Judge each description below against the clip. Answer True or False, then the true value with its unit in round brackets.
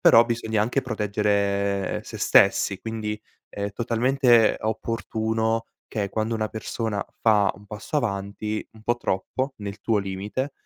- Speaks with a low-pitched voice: True (110 Hz)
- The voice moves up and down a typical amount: False (2.1 semitones)